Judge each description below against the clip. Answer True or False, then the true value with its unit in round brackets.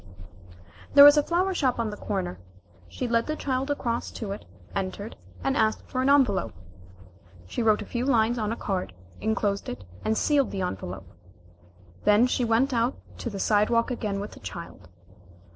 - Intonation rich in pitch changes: False (4.3 semitones)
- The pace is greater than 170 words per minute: True (180 wpm)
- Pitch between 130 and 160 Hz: False (225 Hz)